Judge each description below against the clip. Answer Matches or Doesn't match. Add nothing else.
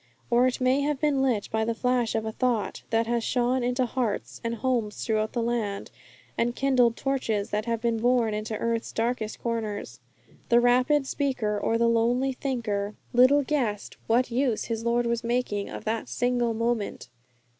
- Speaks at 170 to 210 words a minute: Matches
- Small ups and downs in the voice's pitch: Matches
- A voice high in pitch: Matches